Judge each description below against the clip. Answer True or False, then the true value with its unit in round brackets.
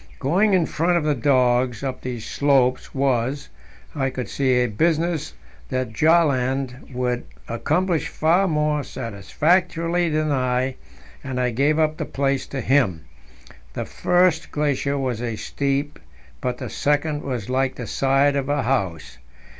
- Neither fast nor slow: True (145 wpm)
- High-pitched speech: False (135 Hz)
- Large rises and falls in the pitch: False (3.4 semitones)